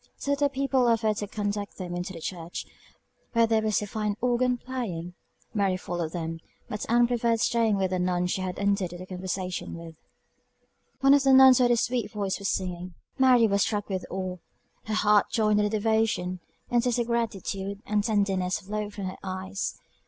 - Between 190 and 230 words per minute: Yes, average, 195 wpm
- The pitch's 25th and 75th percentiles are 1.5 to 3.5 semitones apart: No, average, 3.9 semitones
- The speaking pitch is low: No, high, 205 Hz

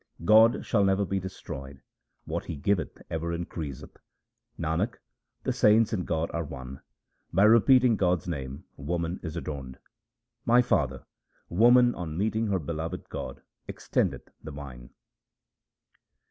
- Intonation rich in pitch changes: Yes, wide, 5.9 semitones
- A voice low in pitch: Yes, very low, 85 Hz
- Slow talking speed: Yes, slow, 130 wpm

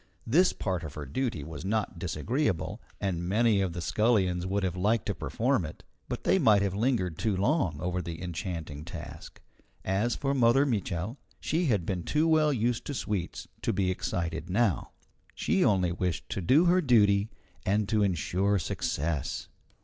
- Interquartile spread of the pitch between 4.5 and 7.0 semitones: Yes, average, 5.2 semitones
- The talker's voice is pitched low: Yes, low, 100 Hz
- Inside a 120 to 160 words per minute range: No, average, 170 wpm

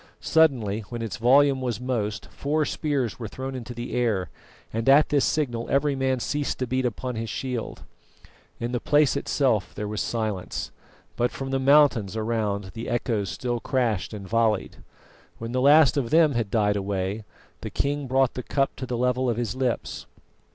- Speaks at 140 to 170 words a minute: No, average, 180 wpm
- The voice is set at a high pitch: No, low, 120 Hz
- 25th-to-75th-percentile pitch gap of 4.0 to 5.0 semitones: No, average, 3.3 semitones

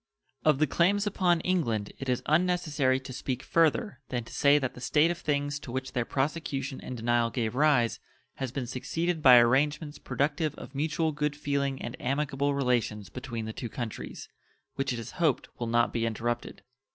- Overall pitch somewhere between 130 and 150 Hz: Yes, low, 135 Hz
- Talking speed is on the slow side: No, average, 185 wpm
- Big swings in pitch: No, average, 3.8 semitones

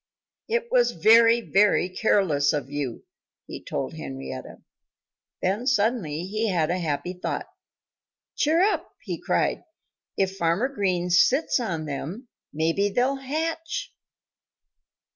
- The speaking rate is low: Yes, slow, 120 wpm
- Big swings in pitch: Yes, wide, 7.5 semitones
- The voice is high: Yes, high, 195 Hz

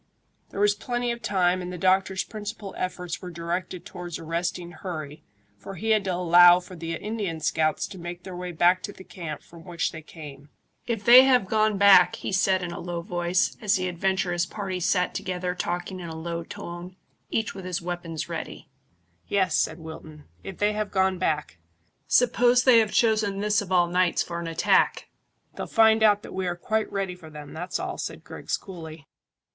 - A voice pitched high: No, medium, 180 Hz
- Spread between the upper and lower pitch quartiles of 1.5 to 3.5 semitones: Yes, average, 2.8 semitones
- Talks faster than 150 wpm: Yes, average, 195 wpm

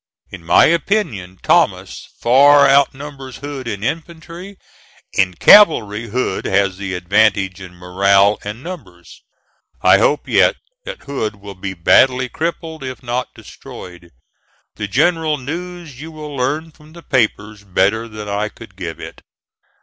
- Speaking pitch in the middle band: No, low, 120 Hz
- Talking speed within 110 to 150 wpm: Yes, average, 140 wpm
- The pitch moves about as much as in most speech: No, wide, 7.4 semitones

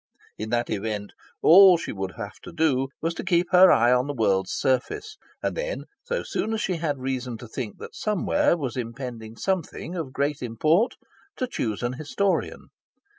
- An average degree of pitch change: No, wide, 7.3 semitones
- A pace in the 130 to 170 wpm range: No, average, 180 wpm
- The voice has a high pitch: No, low, 135 Hz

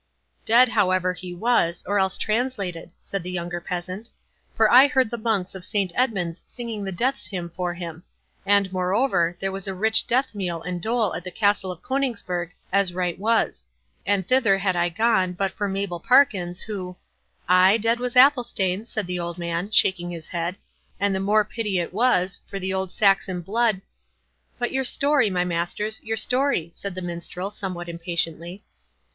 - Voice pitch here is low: No, high, 190 Hz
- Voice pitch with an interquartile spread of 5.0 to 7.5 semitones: No, average, 3.8 semitones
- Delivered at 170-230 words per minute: Yes, average, 175 wpm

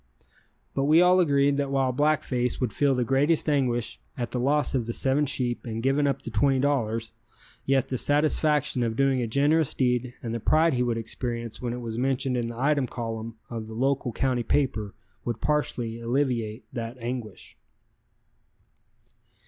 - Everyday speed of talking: Yes, average, 175 wpm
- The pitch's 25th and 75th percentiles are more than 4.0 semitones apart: No, average, 3.2 semitones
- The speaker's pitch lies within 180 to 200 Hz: No, low, 125 Hz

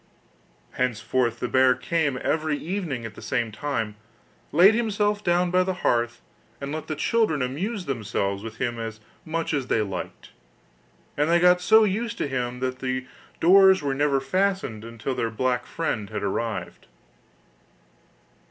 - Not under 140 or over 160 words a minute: Yes, average, 155 wpm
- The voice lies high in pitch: No, medium, 140 Hz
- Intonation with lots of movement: Yes, wide, 7.1 semitones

